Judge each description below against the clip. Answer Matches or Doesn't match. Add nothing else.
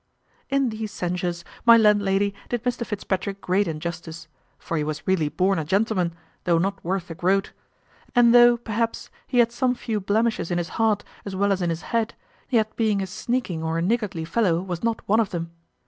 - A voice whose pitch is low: Doesn't match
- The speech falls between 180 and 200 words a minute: Matches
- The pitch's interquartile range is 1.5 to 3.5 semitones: Doesn't match